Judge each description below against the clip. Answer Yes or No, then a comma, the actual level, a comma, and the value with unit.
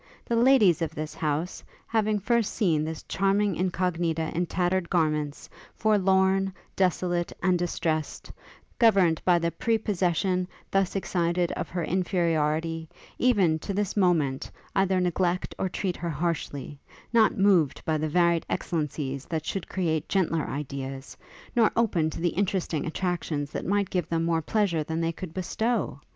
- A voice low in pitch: No, medium, 175 Hz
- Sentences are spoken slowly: No, average, 145 wpm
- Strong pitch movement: No, average, 3.2 semitones